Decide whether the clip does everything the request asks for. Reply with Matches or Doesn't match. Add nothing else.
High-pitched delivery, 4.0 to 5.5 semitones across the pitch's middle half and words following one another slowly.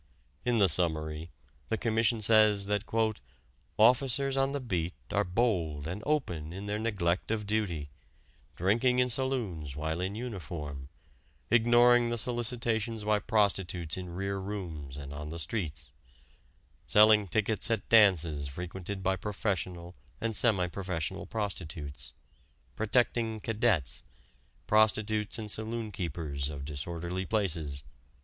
Doesn't match